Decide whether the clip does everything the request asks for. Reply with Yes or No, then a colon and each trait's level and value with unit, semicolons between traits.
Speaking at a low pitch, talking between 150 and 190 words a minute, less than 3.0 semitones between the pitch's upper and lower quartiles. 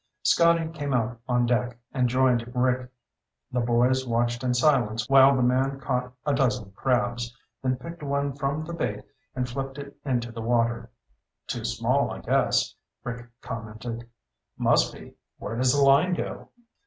Yes: low, 125 Hz; average, 160 wpm; narrow, 2.4 semitones